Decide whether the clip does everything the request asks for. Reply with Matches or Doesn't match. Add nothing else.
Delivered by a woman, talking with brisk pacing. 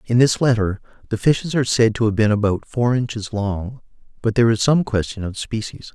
Doesn't match